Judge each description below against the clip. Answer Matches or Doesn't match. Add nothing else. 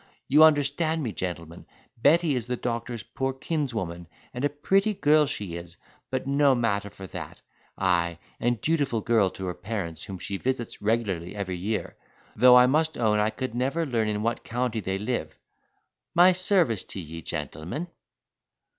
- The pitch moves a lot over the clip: Matches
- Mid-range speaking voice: Doesn't match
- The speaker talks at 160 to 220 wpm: Matches